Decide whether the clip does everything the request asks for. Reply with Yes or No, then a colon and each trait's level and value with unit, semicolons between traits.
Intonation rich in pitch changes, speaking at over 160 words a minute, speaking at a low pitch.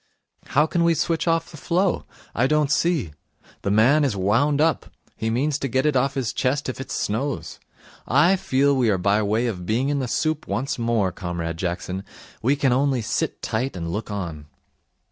Yes: wide, 6.1 semitones; average, 195 wpm; low, 130 Hz